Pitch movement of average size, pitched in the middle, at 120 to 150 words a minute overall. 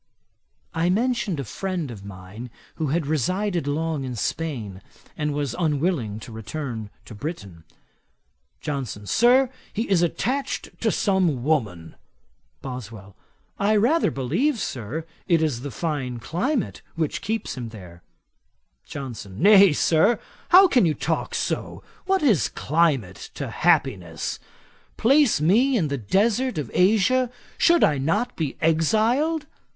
No: wide, 8.9 semitones; medium, 160 Hz; slow, 135 wpm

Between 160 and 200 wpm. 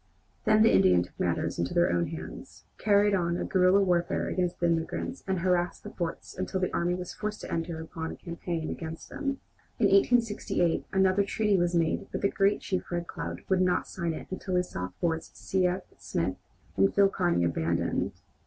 Yes: average, 190 wpm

